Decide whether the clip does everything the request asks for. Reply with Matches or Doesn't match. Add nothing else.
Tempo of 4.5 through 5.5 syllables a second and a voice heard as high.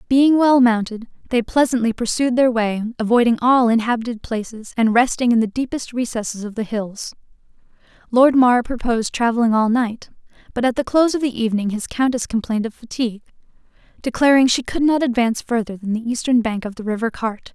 Doesn't match